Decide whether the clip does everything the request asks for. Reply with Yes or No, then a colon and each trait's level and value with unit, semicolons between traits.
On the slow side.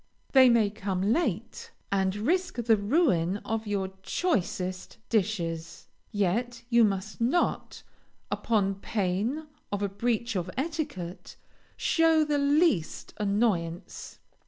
Yes: slow, 110 wpm